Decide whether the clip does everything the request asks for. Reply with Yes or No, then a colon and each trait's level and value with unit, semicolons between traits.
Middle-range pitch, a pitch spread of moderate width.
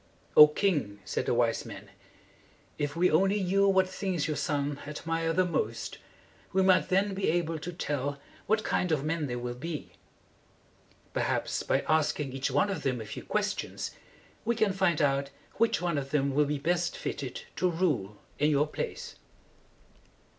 Yes: medium, 155 Hz; average, 4.6 semitones